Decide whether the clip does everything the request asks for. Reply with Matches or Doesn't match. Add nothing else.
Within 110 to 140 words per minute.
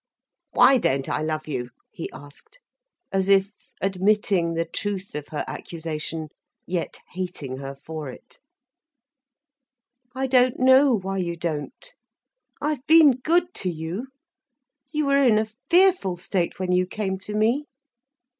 Matches